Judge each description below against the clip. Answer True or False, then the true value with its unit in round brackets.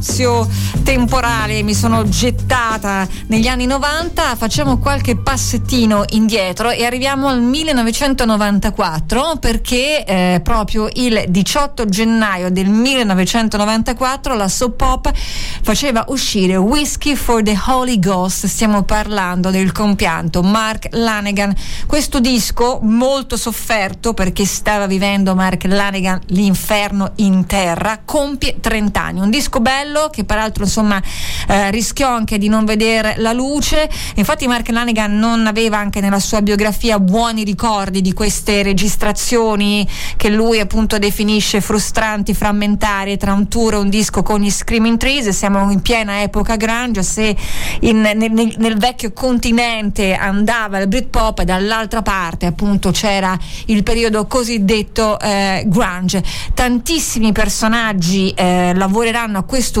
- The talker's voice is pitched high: True (215 Hz)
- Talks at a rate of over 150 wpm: False (130 wpm)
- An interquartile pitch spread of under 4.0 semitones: True (2.9 semitones)